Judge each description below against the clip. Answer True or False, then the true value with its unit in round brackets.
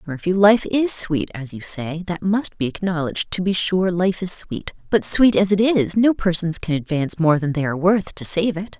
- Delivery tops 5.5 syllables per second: False (5.0 syllables/s)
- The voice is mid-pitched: True (180 Hz)